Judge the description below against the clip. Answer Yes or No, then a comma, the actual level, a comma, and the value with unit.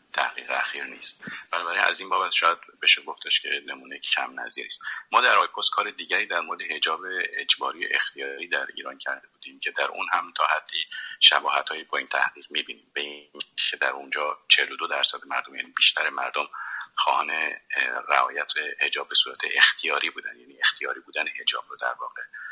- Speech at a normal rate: No, fast, 180 wpm